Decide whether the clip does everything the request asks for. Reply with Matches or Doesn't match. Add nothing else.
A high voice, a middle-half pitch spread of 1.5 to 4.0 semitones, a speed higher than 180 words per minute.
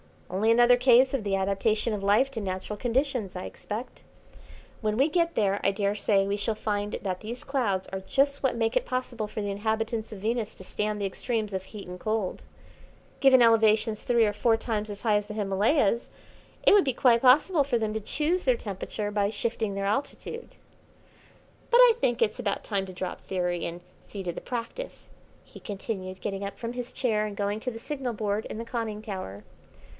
Matches